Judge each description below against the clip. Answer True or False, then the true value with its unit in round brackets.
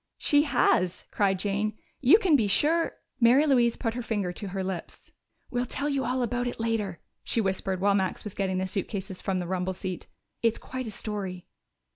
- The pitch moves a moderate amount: True (4.5 semitones)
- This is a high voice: True (210 Hz)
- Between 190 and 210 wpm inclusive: True (200 wpm)